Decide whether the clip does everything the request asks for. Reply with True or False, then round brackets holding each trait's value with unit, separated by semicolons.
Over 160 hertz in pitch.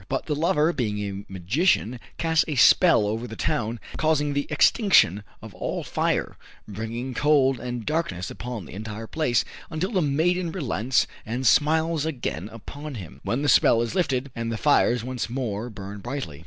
False (125 Hz)